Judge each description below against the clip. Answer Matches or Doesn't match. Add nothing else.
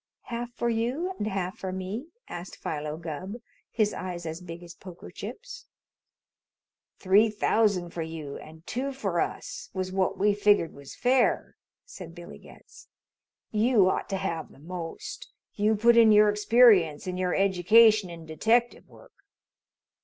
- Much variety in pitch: Doesn't match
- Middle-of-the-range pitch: Doesn't match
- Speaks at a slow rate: Doesn't match